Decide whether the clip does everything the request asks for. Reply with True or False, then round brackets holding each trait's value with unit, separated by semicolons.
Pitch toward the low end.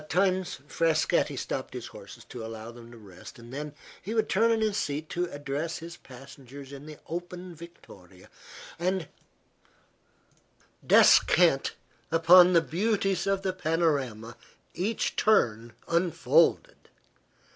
False (165 Hz)